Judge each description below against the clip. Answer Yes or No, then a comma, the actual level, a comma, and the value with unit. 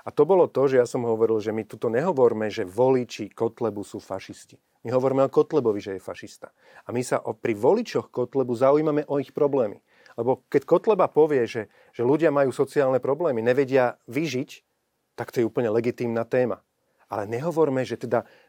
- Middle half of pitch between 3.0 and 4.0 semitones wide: Yes, average, 3.5 semitones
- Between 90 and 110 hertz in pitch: No, low, 125 Hz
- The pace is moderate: No, fast, 185 wpm